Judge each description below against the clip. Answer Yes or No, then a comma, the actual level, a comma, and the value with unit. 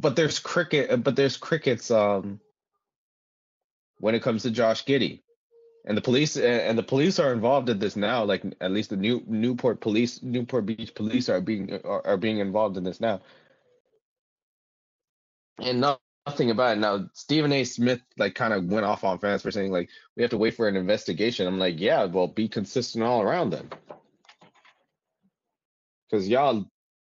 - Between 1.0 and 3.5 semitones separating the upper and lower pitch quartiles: No, average, 4.7 semitones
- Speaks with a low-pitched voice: Yes, low, 115 Hz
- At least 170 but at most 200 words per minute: Yes, average, 175 wpm